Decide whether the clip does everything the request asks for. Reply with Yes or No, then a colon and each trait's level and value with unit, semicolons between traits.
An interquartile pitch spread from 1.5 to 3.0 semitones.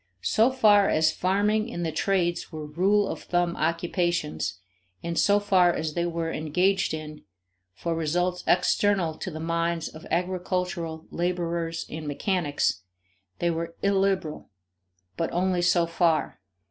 Yes: narrow, 2.4 semitones